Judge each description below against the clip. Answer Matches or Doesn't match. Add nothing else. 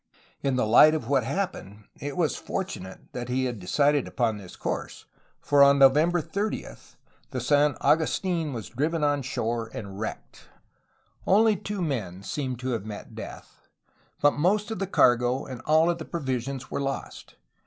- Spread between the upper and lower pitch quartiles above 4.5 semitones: Matches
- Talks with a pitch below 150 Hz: Matches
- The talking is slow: Doesn't match